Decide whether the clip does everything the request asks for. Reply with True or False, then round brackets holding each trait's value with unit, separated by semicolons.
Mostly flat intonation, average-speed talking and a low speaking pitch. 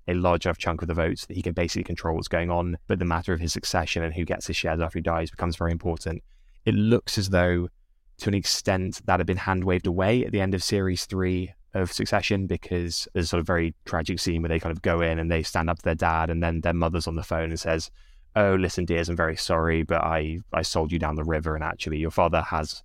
False (2.0 semitones; 270 wpm; 85 Hz)